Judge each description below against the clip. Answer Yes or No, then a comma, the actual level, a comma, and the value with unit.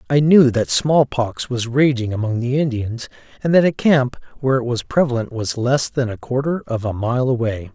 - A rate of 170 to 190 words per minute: No, average, 200 wpm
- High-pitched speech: No, low, 125 Hz